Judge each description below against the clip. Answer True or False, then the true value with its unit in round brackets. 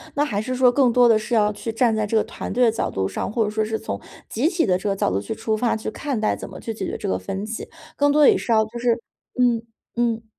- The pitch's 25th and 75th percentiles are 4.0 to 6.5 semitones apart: False (2.4 semitones)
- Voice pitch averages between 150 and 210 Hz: False (225 Hz)